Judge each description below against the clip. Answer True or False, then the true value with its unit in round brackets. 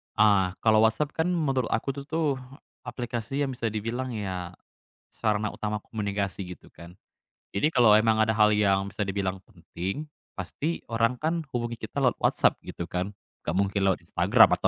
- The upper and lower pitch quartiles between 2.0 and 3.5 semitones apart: False (4.1 semitones)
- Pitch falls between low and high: False (110 Hz)